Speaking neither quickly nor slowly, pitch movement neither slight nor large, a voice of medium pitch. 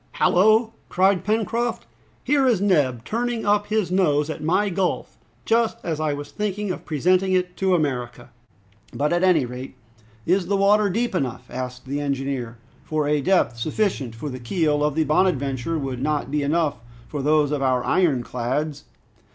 No: average, 170 wpm; wide, 6.0 semitones; medium, 155 Hz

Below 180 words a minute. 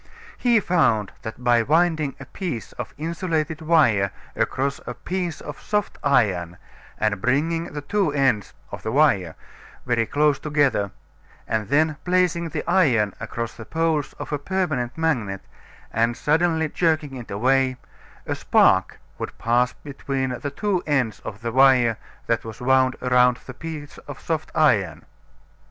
Yes: average, 150 wpm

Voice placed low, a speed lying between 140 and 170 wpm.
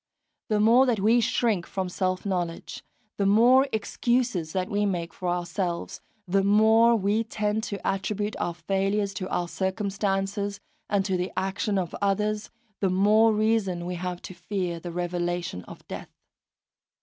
No: high, 195 Hz; average, 160 wpm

